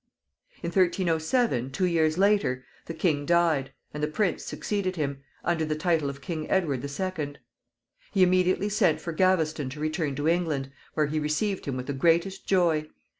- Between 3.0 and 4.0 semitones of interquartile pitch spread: Yes, average, 3.7 semitones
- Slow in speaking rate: No, average, 175 wpm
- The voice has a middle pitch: Yes, medium, 160 Hz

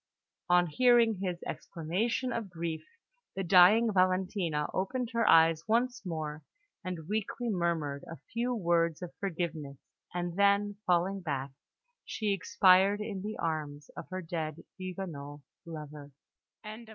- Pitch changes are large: No, average, 4.0 semitones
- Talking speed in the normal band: No, slow, 125 wpm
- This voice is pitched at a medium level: Yes, medium, 180 Hz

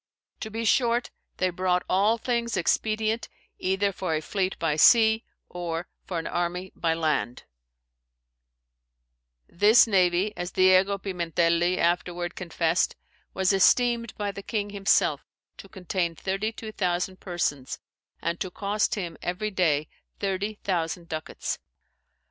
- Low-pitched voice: No, medium, 185 Hz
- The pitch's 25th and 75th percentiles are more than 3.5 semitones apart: No, average, 3.2 semitones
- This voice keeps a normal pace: No, slow, 125 wpm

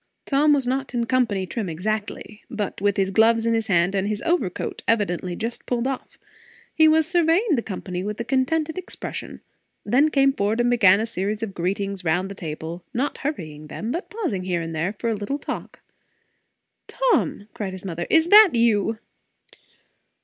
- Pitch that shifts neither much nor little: No, wide, 6.1 semitones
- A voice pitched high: Yes, high, 220 Hz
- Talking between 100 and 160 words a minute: No, average, 180 wpm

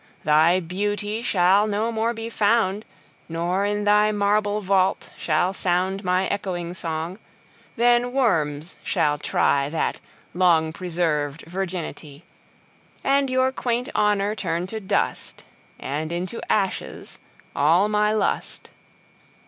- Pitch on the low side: No, high, 190 Hz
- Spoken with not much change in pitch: No, average, 3.9 semitones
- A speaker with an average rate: No, slow, 100 wpm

